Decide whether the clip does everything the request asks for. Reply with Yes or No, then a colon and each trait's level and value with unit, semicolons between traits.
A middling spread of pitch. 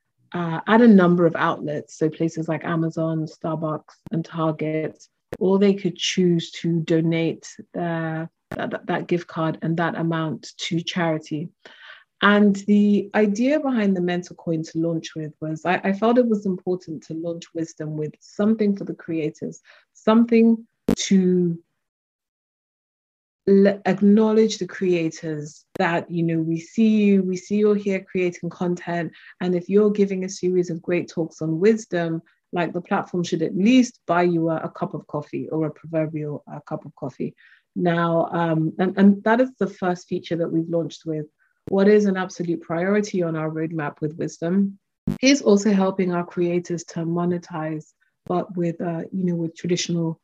Yes: average, 3.1 semitones